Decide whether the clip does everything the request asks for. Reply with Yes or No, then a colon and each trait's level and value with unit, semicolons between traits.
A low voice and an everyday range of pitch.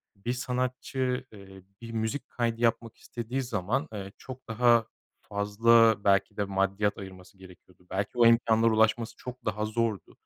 Yes: low, 110 Hz; average, 3.0 semitones